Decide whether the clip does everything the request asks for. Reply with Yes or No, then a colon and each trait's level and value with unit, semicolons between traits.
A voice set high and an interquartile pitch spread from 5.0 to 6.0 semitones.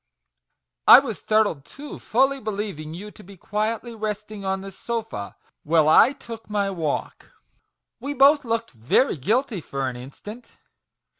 Yes: high, 210 Hz; wide, 5.6 semitones